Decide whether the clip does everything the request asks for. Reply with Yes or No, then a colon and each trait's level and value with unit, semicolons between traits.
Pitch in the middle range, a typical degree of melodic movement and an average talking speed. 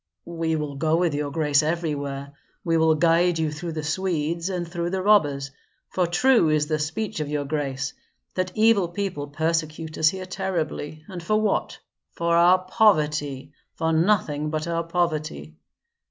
Yes: medium, 160 Hz; average, 3.0 semitones; average, 165 wpm